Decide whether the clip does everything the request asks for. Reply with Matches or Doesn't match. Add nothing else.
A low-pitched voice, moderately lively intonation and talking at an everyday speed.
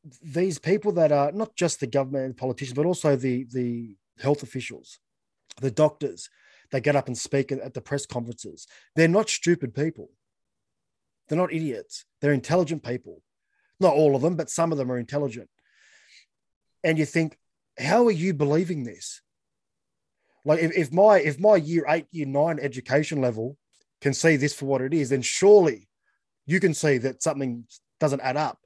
Doesn't match